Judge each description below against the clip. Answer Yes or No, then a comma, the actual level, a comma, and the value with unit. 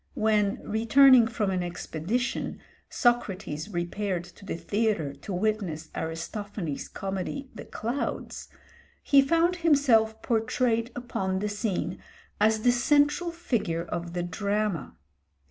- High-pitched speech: Yes, high, 215 Hz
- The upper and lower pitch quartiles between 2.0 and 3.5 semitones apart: No, average, 5.0 semitones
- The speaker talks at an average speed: No, slow, 115 wpm